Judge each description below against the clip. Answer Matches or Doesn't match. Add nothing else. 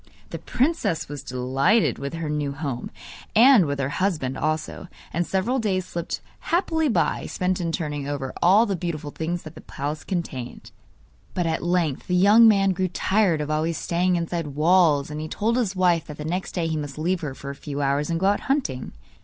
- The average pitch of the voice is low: Doesn't match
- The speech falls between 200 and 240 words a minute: Matches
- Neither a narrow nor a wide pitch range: Matches